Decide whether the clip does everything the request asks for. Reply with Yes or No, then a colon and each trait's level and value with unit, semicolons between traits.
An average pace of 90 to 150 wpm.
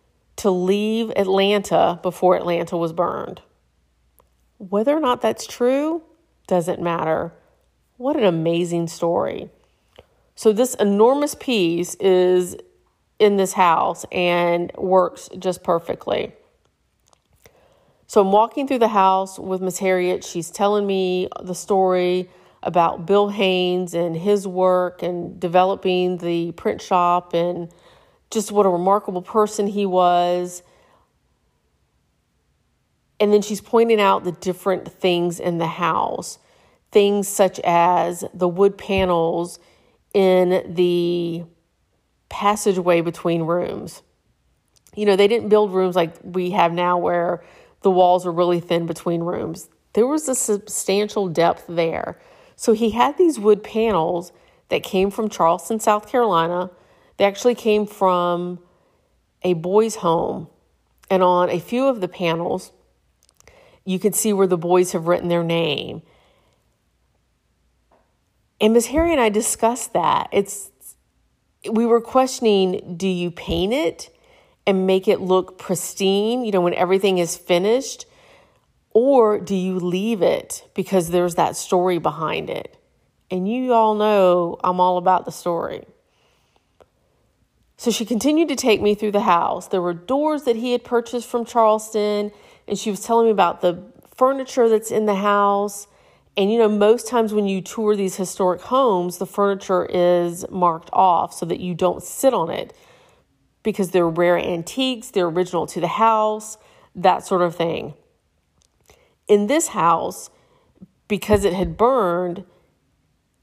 Yes: average, 140 wpm